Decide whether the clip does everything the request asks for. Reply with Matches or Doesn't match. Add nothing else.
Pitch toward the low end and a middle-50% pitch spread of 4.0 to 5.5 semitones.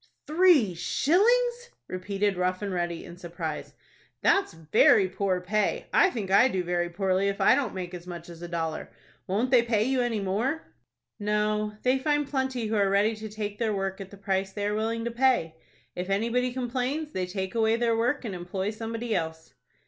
Doesn't match